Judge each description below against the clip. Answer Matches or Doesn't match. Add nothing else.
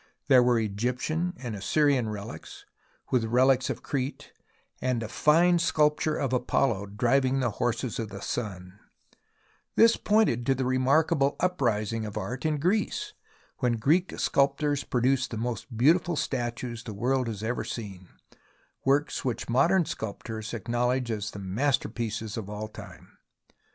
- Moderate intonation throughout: Matches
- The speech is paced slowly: Doesn't match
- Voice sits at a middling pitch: Doesn't match